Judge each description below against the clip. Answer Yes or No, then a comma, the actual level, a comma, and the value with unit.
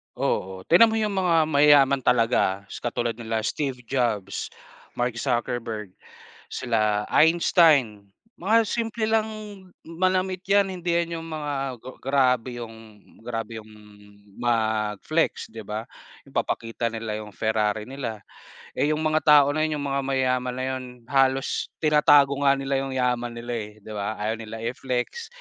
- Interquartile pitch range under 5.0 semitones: No, wide, 5.4 semitones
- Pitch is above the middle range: No, low, 130 Hz